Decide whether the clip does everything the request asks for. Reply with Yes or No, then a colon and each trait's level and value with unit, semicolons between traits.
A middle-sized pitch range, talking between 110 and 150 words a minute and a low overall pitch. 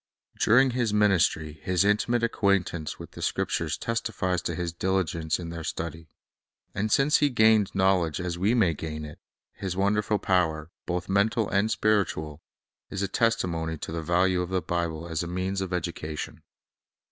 No: average, 3.9 semitones; average, 165 wpm; very low, 90 Hz